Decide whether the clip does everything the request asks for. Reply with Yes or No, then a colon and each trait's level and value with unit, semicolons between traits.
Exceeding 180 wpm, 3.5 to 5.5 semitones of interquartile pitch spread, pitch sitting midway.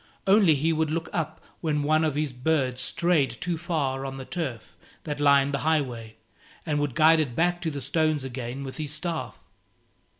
No: average, 190 wpm; average, 3.1 semitones; medium, 150 Hz